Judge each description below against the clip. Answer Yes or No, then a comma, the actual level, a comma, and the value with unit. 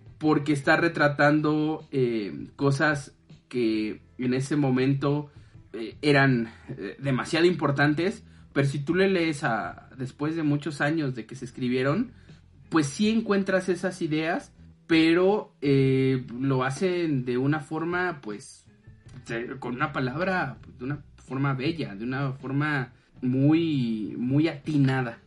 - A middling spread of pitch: Yes, average, 4.0 semitones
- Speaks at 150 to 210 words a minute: No, average, 130 wpm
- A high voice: No, medium, 140 Hz